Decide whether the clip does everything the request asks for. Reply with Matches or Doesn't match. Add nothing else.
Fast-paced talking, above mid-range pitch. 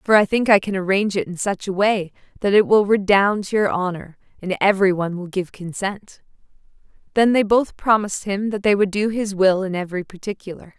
Matches